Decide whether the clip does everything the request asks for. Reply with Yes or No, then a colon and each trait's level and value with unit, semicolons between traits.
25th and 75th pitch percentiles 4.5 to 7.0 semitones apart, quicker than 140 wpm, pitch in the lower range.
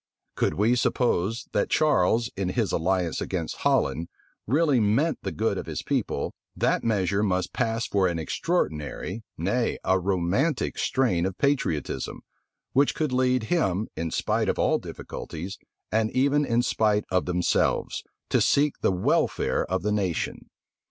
Yes: wide, 5.6 semitones; average, 150 wpm; low, 105 Hz